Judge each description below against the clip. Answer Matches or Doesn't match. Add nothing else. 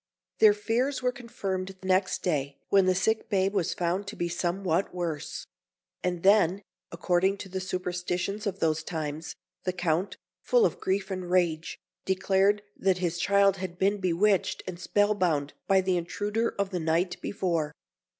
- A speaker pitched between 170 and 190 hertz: Matches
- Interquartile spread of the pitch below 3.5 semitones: Matches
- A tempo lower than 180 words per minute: Matches